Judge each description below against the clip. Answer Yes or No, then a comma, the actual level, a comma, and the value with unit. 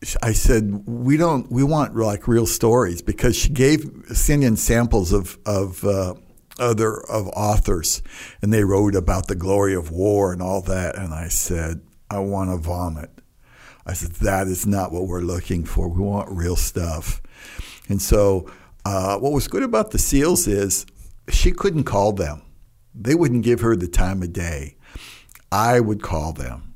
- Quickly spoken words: No, average, 175 wpm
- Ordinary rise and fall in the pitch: Yes, average, 4.1 semitones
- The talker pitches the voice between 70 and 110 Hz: Yes, low, 100 Hz